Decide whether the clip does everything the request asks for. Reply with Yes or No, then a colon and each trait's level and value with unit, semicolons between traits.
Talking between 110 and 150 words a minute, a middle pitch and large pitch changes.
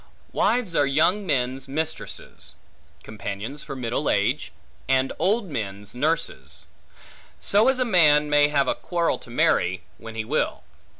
Yes: average, 140 wpm; medium, 145 Hz; wide, 5.7 semitones